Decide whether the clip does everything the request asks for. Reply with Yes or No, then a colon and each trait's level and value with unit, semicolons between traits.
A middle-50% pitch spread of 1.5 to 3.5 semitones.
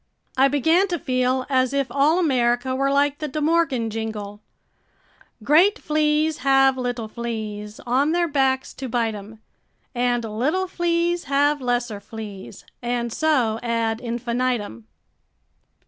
No: average, 4.2 semitones